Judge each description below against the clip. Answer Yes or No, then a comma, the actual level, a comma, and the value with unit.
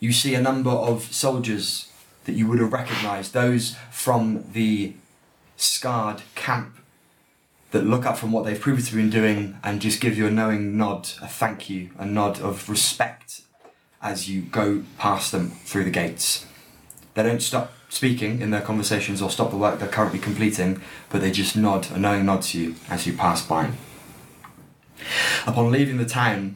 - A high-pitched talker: No, low, 105 Hz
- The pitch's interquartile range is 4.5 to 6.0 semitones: No, average, 2.9 semitones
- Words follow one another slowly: No, average, 175 wpm